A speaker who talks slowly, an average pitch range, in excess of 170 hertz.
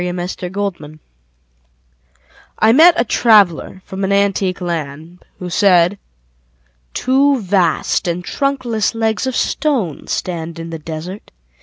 Yes: slow, 125 wpm; average, 4.6 semitones; high, 190 Hz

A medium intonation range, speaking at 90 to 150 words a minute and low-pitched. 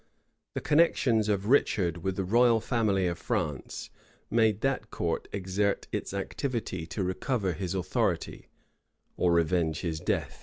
Yes: average, 4.3 semitones; average, 140 wpm; very low, 95 Hz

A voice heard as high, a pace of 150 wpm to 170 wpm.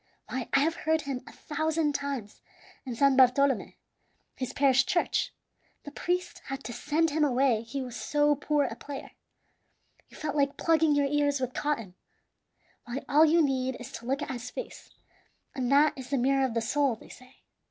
No: very high, 275 Hz; average, 185 wpm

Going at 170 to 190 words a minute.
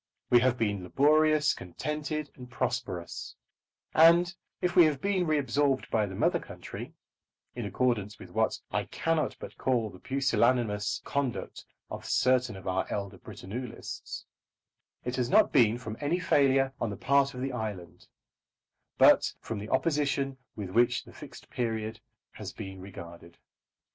No: average, 150 wpm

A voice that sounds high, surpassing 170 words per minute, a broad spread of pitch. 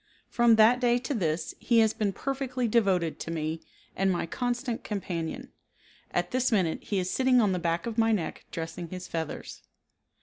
Yes: high, 210 Hz; average, 180 wpm; wide, 6.0 semitones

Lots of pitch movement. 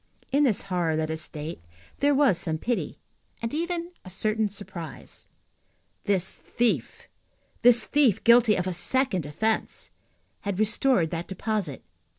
Yes: wide, 5.9 semitones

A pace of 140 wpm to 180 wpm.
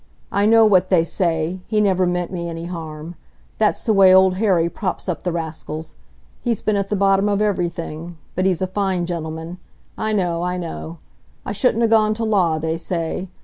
No: average, 190 wpm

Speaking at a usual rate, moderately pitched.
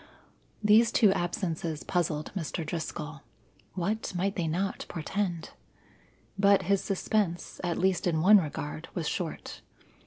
No: slow, 125 wpm; medium, 175 Hz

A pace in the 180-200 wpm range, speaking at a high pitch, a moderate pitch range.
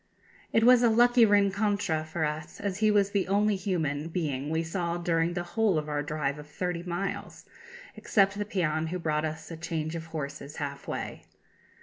No: average, 190 wpm; medium, 170 Hz; average, 4.5 semitones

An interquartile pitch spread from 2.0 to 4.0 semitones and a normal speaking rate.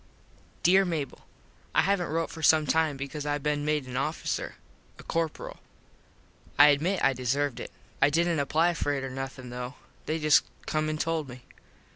Yes: average, 2.9 semitones; average, 175 wpm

